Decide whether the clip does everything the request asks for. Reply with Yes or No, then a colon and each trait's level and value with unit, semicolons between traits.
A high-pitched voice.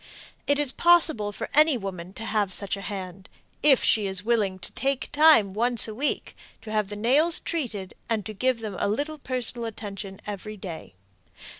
Yes: high, 215 Hz